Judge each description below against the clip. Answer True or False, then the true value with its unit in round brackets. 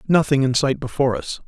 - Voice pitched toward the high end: False (140 Hz)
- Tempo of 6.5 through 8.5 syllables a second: False (6.3 syllables/s)